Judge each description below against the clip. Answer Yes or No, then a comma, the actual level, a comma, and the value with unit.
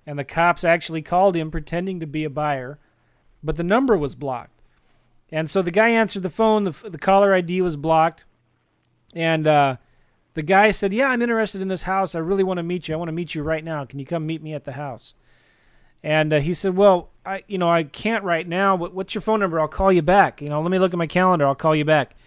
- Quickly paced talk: Yes, fast, 255 wpm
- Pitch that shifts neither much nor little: Yes, average, 3.8 semitones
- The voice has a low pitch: No, medium, 170 Hz